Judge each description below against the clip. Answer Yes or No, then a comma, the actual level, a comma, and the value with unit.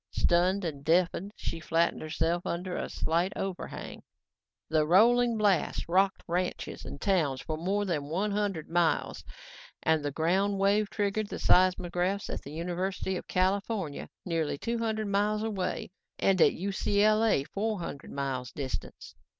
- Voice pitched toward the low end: No, medium, 185 Hz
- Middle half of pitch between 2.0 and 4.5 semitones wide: Yes, average, 3.7 semitones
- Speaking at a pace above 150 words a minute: No, average, 145 wpm